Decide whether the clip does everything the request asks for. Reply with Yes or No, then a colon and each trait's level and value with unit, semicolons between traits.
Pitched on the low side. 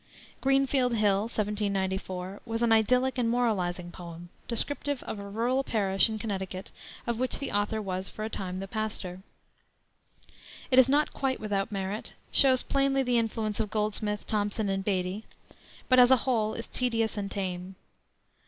No: high, 215 Hz